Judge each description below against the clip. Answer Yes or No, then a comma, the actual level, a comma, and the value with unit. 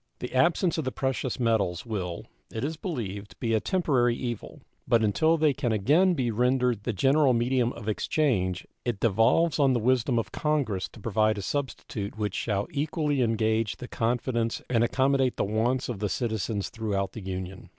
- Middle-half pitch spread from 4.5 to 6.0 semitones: No, average, 3.8 semitones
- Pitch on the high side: No, low, 120 Hz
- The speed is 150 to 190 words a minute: Yes, average, 180 wpm